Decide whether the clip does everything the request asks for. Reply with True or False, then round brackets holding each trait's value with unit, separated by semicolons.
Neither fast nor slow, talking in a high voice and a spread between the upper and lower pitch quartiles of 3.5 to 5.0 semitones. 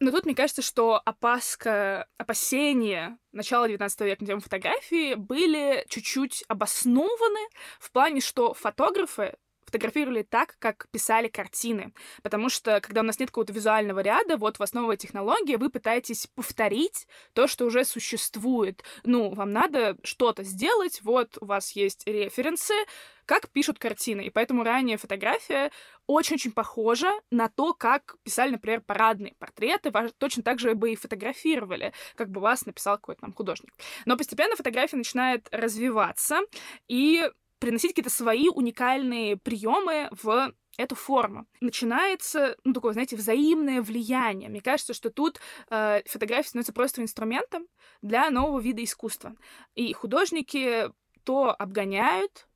True (140 wpm; 240 Hz; 3.9 semitones)